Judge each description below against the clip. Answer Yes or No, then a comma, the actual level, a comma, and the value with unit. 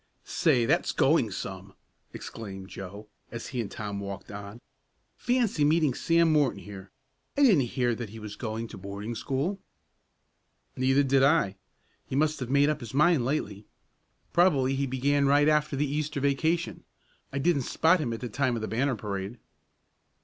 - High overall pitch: No, low, 130 Hz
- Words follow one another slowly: No, average, 170 wpm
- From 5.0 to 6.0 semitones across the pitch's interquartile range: Yes, wide, 5.6 semitones